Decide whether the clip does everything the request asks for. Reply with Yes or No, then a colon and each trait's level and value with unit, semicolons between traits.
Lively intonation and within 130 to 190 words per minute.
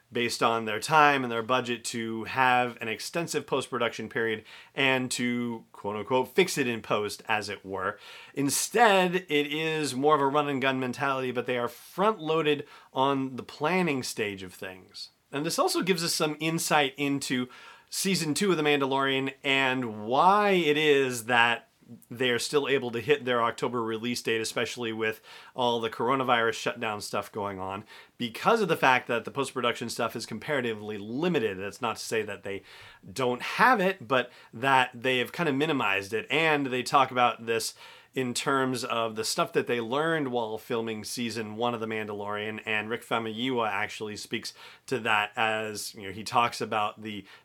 No: average, 3.8 semitones; average, 180 wpm